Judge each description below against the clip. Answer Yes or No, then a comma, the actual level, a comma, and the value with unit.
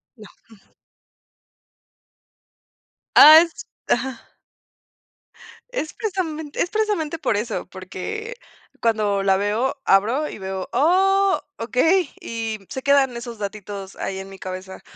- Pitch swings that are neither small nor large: No, wide, 8.1 semitones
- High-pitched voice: Yes, high, 235 Hz